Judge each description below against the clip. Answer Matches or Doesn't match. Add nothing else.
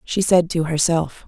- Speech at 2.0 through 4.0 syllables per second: Doesn't match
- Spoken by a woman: Matches